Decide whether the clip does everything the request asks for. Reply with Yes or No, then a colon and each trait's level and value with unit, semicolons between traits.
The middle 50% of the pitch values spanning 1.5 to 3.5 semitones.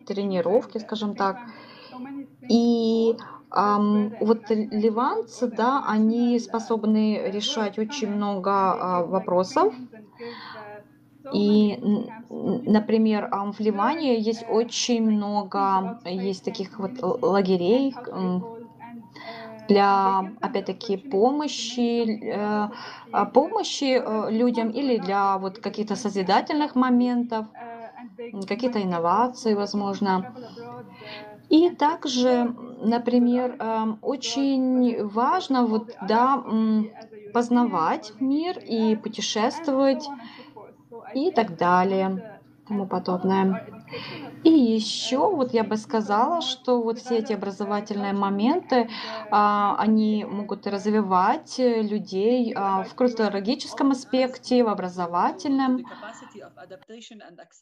Yes: average, 3.1 semitones